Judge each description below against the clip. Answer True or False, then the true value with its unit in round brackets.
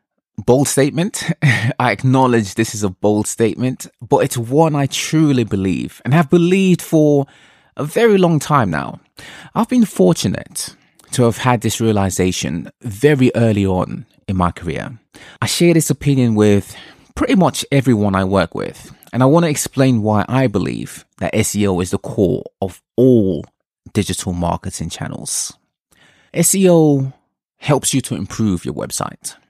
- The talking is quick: False (150 wpm)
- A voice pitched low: True (125 Hz)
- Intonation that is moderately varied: False (6.2 semitones)